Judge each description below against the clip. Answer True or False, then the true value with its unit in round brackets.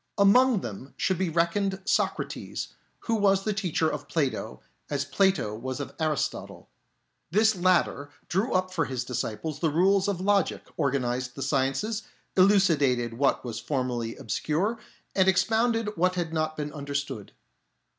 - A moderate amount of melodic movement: False (6.2 semitones)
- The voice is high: False (165 Hz)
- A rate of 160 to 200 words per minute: False (145 wpm)